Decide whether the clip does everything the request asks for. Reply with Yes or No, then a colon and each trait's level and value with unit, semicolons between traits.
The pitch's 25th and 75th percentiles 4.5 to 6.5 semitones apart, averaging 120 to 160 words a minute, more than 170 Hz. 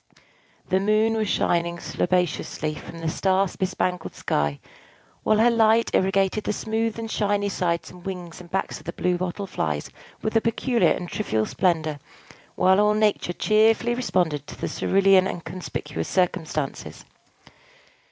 No: average, 3.8 semitones; average, 150 wpm; high, 190 Hz